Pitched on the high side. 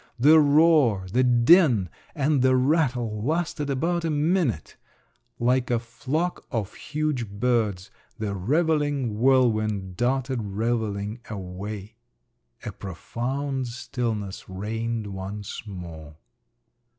No: low, 120 Hz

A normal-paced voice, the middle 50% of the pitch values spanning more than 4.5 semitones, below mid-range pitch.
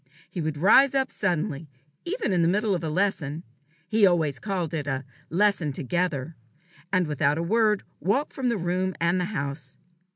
No: average, 175 wpm; average, 5.0 semitones; medium, 175 Hz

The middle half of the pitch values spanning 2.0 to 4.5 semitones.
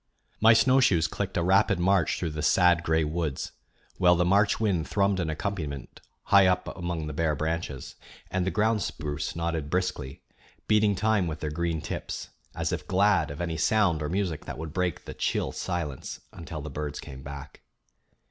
Yes: average, 3.9 semitones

